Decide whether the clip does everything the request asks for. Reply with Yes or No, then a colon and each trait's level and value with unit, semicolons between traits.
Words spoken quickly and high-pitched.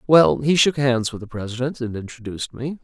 No: fast, 210 wpm; low, 125 Hz